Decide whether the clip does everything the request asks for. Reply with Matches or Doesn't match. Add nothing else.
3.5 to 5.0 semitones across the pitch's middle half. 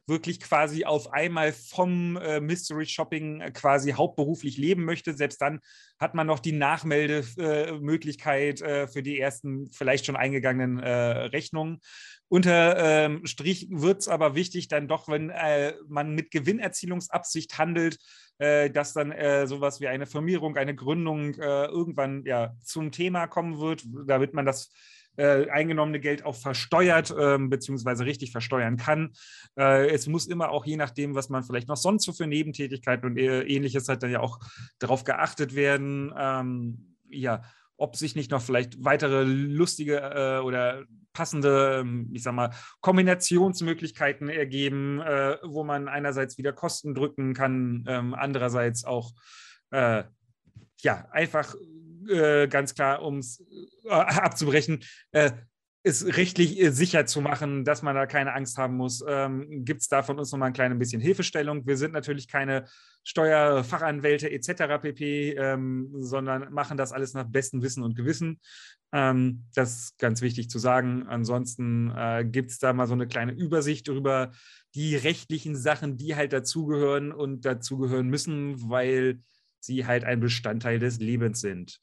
Doesn't match